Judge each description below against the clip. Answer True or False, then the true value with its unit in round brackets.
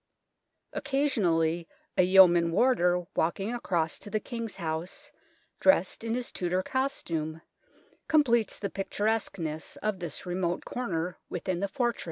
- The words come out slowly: True (130 wpm)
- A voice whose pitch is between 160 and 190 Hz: True (185 Hz)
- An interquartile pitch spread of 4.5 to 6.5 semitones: True (5.1 semitones)